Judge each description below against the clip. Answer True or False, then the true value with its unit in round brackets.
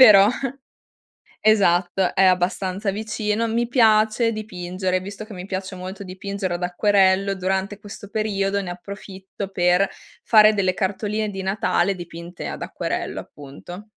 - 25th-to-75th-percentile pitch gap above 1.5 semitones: True (2.4 semitones)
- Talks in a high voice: True (195 Hz)